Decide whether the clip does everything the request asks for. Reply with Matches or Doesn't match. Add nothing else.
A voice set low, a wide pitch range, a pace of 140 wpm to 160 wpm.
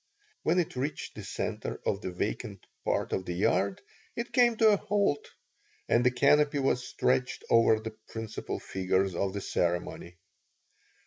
Matches